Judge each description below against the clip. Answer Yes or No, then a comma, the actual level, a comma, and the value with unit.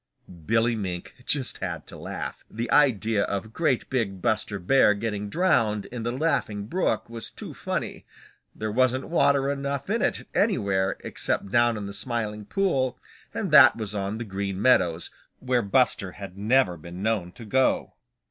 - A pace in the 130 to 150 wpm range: No, average, 165 wpm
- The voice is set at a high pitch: No, low, 115 Hz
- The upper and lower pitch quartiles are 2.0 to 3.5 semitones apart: No, average, 4.5 semitones